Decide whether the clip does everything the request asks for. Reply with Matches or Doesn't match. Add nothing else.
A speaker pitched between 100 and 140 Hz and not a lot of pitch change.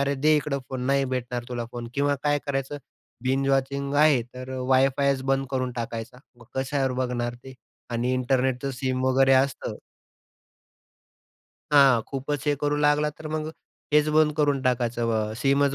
Matches